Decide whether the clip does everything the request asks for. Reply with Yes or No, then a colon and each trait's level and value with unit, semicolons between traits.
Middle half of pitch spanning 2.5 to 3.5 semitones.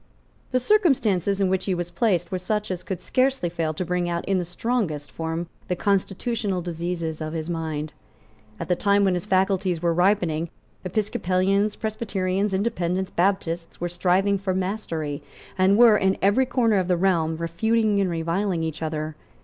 Yes: average, 3.0 semitones